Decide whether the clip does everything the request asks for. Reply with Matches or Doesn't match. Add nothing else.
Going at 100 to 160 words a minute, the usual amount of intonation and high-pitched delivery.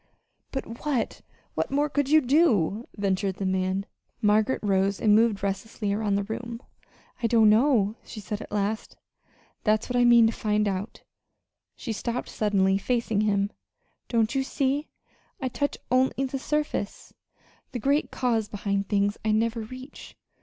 Matches